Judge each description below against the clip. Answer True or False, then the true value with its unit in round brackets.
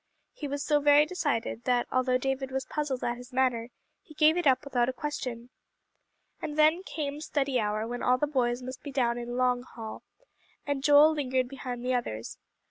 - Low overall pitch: False (260 Hz)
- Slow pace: False (195 wpm)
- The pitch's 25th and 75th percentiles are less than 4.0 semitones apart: True (3.0 semitones)